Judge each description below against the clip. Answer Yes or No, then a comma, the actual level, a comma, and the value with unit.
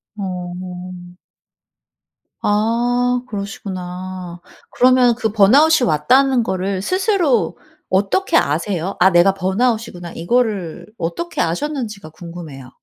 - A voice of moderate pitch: No, high, 195 Hz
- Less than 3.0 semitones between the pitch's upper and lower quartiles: No, wide, 5.5 semitones